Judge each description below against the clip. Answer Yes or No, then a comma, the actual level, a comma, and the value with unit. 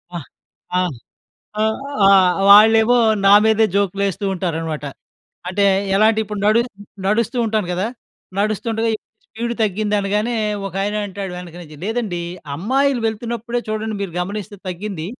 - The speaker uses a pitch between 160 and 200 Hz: No, high, 210 Hz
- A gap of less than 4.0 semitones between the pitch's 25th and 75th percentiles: Yes, average, 2.8 semitones